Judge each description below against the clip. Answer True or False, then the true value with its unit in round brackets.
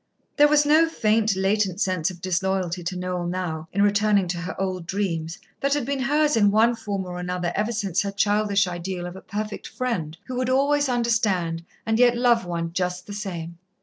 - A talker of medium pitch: False (200 Hz)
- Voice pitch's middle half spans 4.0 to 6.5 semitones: True (4.3 semitones)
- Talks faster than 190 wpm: True (200 wpm)